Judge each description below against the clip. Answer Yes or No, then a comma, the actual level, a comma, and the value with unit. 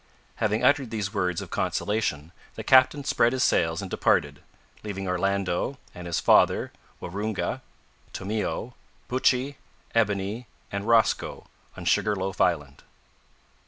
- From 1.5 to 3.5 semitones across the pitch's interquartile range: No, average, 4.2 semitones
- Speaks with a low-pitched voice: Yes, low, 100 Hz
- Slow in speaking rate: Yes, slow, 125 wpm